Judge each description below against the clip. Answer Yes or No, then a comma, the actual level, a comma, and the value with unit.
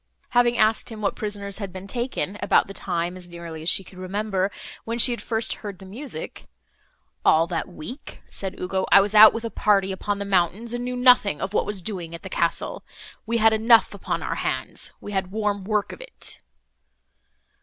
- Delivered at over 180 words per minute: Yes, fast, 205 wpm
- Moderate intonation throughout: Yes, average, 3.2 semitones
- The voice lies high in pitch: Yes, high, 200 Hz